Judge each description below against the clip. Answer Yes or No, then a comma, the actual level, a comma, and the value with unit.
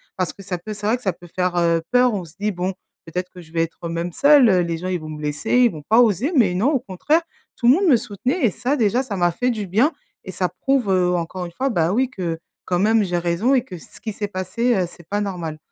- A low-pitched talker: No, high, 190 Hz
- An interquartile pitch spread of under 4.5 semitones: No, wide, 5.4 semitones